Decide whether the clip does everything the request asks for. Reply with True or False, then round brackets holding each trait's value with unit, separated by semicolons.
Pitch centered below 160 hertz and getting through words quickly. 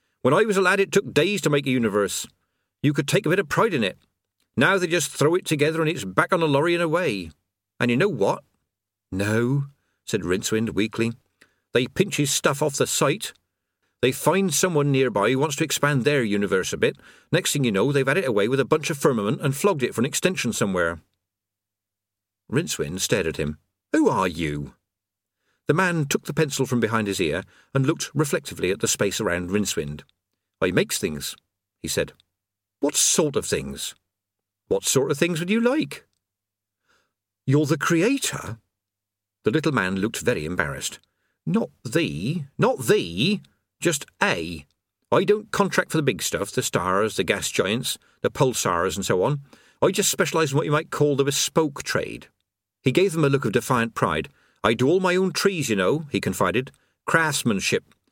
False (135 Hz; 190 wpm)